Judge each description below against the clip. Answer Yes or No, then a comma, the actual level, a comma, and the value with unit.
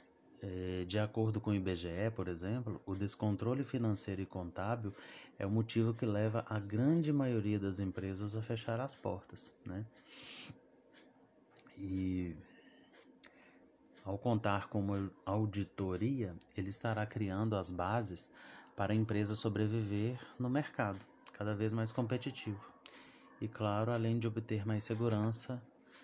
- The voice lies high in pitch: No, low, 105 Hz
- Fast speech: No, average, 130 wpm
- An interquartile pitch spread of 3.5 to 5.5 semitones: No, average, 2.7 semitones